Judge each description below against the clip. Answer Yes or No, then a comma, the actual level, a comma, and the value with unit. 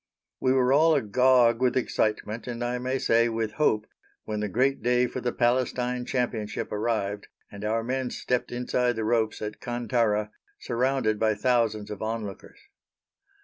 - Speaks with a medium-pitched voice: No, low, 120 Hz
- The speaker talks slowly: No, average, 155 wpm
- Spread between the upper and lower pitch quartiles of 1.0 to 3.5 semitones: Yes, narrow, 2.6 semitones